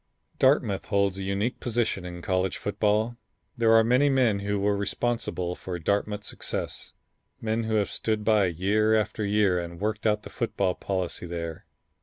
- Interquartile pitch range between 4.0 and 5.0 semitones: No, average, 2.7 semitones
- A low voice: Yes, low, 105 Hz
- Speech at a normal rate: Yes, average, 165 wpm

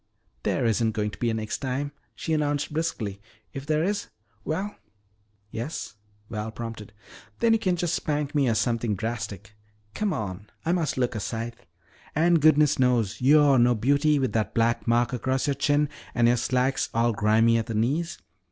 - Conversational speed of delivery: Yes, average, 180 wpm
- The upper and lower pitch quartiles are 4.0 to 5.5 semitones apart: Yes, average, 4.9 semitones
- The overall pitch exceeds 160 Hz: No, low, 125 Hz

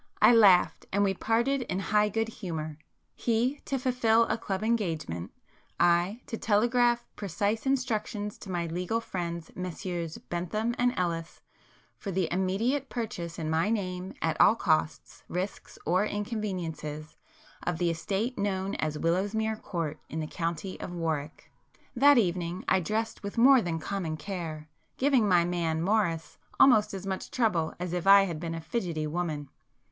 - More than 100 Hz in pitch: Yes, high, 190 Hz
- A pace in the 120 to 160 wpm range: Yes, average, 155 wpm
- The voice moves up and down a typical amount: Yes, average, 4.7 semitones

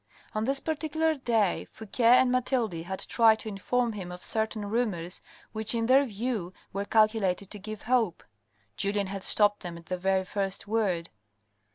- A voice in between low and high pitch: No, high, 215 Hz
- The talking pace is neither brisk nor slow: Yes, average, 170 wpm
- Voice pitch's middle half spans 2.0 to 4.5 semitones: Yes, average, 3.8 semitones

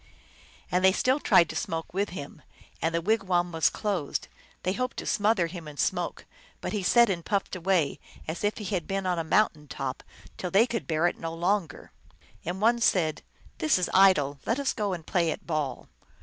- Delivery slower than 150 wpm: No, fast, 205 wpm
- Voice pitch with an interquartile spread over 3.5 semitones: Yes, average, 3.9 semitones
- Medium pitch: Yes, medium, 180 Hz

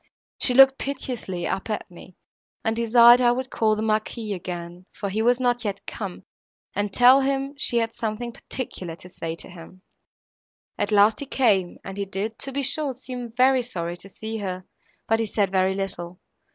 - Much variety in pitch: No, average, 4.5 semitones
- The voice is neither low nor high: No, high, 220 Hz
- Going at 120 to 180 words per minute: No, average, 190 wpm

